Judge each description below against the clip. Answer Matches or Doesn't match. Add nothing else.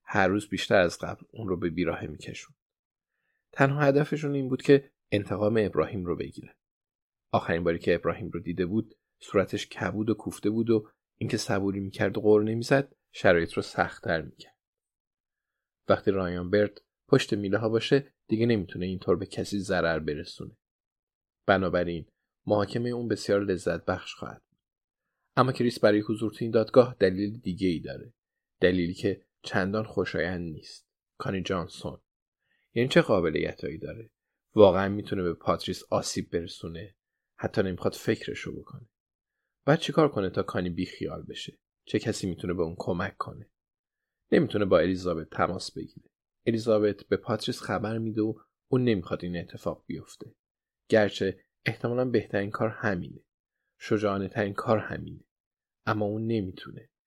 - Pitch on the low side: Matches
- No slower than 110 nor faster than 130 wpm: Doesn't match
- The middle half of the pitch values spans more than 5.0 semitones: Doesn't match